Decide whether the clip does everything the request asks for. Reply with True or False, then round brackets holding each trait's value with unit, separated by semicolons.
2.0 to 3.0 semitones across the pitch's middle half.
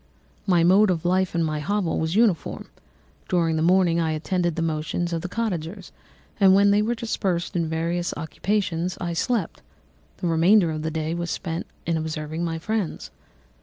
True (2.7 semitones)